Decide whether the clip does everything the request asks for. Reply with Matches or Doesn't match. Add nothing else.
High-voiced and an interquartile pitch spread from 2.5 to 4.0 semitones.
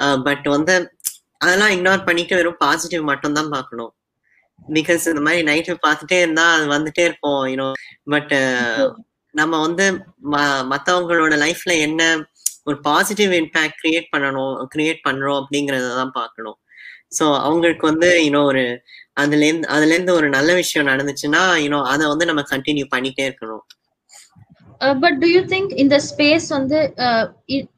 Doesn't match